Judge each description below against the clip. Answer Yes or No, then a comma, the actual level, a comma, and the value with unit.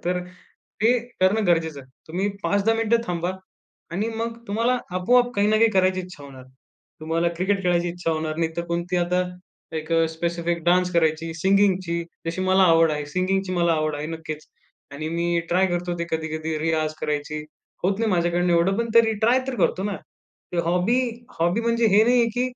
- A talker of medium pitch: Yes, medium, 175 Hz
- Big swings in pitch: No, average, 3.5 semitones